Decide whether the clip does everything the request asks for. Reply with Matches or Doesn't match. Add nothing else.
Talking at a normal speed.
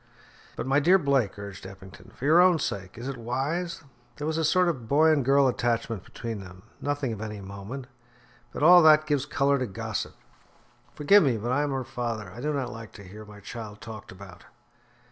Doesn't match